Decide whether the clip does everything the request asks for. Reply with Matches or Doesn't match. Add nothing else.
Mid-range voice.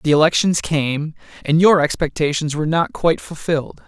Matches